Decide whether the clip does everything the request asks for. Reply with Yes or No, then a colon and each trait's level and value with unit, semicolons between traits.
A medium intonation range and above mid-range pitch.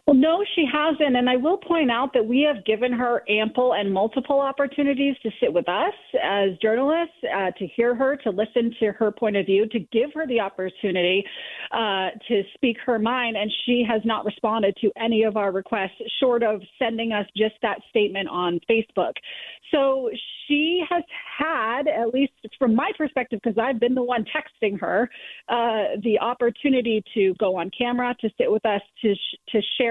Yes: average, 4.0 semitones; high, 230 Hz